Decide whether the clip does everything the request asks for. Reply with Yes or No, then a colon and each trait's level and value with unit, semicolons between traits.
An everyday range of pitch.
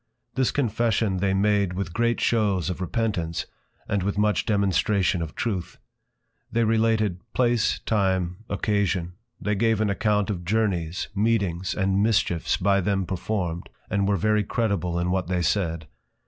Yes: average, 3.0 semitones